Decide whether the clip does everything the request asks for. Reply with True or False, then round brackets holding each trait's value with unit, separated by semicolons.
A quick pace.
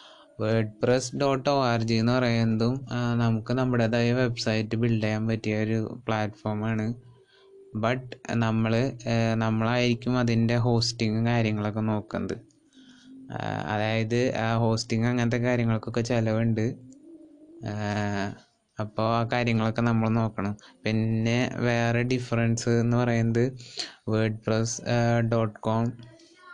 False (95 wpm)